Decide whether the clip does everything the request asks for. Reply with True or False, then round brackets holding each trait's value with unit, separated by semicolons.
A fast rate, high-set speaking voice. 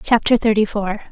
False (160 wpm; 215 Hz)